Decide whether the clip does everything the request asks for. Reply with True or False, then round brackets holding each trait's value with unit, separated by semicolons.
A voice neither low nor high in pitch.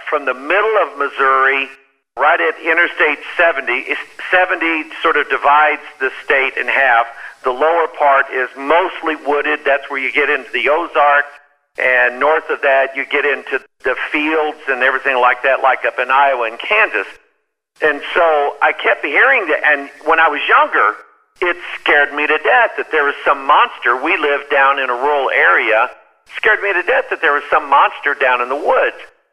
True (145 Hz)